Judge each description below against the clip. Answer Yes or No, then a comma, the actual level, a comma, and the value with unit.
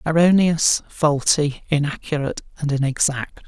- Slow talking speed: Yes, slow, 85 wpm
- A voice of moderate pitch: Yes, medium, 150 Hz